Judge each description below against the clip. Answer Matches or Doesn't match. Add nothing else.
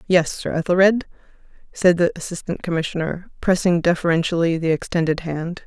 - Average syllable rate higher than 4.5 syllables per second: Matches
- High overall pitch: Doesn't match